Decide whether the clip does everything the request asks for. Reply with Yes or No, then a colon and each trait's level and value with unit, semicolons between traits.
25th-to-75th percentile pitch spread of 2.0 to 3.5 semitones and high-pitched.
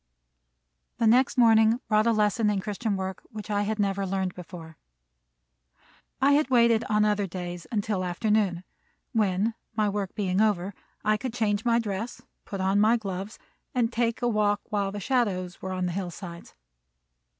Yes: average, 2.9 semitones; high, 205 Hz